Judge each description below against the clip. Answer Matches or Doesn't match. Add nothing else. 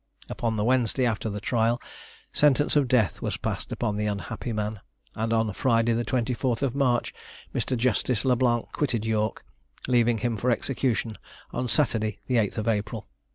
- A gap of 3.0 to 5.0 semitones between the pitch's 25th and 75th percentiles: Doesn't match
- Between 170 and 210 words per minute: Doesn't match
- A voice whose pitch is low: Matches